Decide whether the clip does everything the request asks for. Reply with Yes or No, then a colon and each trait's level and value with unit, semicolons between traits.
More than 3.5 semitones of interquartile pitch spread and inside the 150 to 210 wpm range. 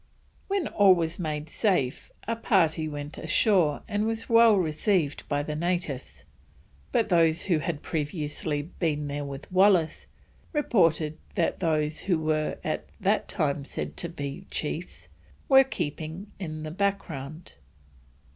No: average, 4.3 semitones; slow, 135 wpm